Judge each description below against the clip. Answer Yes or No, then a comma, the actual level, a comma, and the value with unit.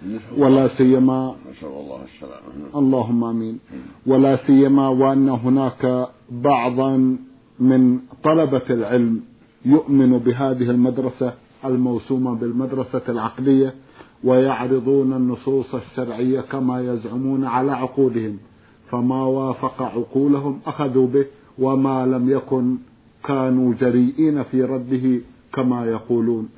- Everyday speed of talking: Yes, average, 90 wpm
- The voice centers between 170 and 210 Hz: No, low, 130 Hz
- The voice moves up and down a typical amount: No, narrow, 1.3 semitones